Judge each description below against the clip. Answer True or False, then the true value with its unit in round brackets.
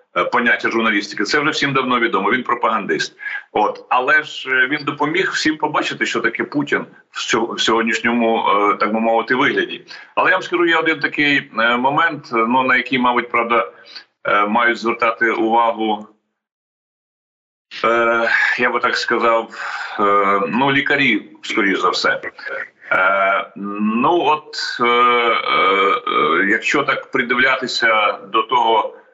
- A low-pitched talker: True (130 Hz)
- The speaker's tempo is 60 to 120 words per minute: True (115 wpm)